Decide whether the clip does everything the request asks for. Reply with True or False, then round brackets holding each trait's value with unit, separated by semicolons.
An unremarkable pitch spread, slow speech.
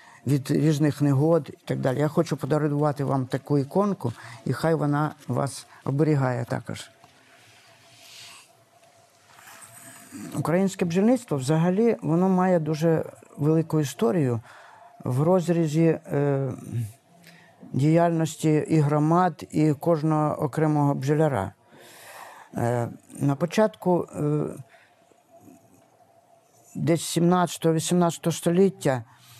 True (3.2 semitones; 90 wpm)